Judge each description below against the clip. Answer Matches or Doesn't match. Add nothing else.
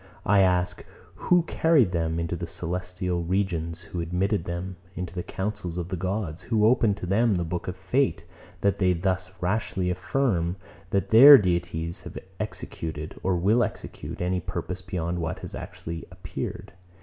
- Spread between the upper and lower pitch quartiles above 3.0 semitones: Doesn't match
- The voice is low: Matches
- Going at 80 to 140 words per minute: Doesn't match